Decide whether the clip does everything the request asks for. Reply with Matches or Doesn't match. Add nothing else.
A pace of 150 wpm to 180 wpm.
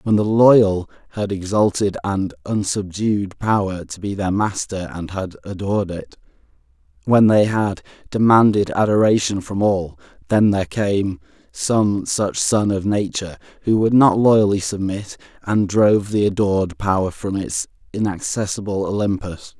Doesn't match